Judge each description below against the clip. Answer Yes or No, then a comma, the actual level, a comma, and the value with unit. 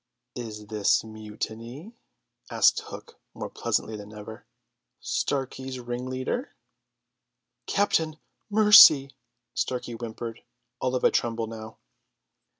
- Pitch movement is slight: No, average, 3.3 semitones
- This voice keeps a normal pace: No, slow, 95 wpm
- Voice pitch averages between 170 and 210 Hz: No, low, 120 Hz